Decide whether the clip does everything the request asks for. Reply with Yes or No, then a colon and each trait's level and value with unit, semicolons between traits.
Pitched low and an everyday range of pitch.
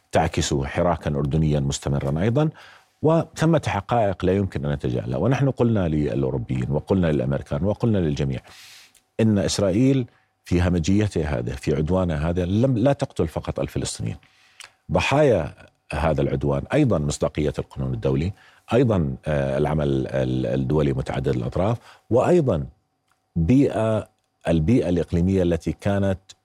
No: very low, 85 Hz; wide, 6.8 semitones